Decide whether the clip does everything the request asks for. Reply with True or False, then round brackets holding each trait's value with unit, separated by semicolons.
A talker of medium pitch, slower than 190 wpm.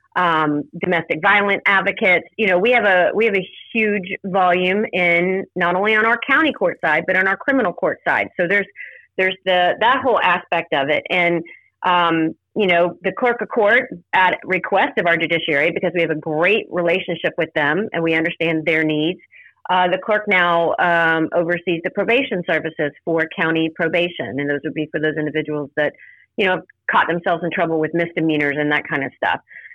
False (175 Hz; 195 wpm)